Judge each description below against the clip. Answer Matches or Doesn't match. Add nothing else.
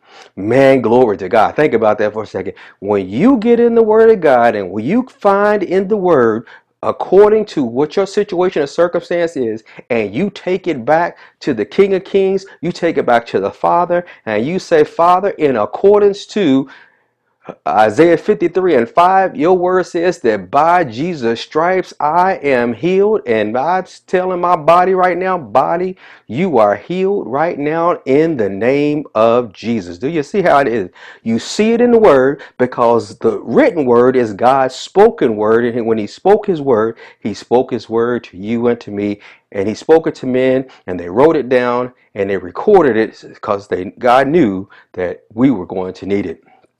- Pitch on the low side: Doesn't match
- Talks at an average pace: Matches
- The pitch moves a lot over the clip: Matches